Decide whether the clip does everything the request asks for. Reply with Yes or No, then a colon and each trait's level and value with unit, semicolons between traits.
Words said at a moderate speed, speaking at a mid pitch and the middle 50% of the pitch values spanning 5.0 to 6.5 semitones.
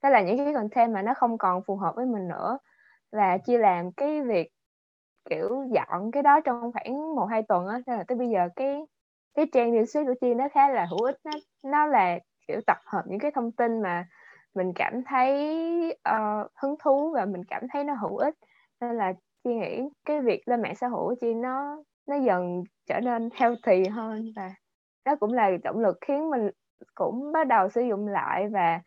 No: average, 210 wpm; high, 240 Hz; average, 5.3 semitones